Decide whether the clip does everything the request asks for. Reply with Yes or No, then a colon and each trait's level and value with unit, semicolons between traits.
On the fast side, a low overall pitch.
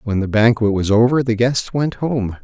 Yes: fast, 220 wpm; low, 115 Hz